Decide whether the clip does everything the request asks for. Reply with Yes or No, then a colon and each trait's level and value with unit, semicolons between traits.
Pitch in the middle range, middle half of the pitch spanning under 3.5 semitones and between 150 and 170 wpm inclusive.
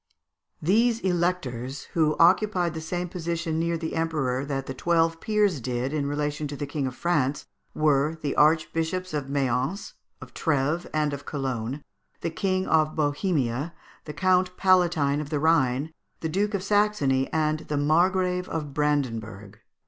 No: medium, 155 Hz; average, 3.8 semitones; average, 155 wpm